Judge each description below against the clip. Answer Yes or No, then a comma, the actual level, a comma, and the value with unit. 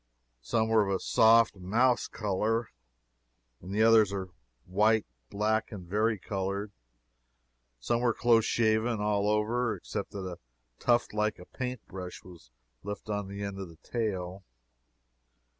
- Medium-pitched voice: No, low, 105 Hz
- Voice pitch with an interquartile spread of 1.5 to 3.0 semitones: Yes, average, 2.7 semitones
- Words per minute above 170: No, average, 145 wpm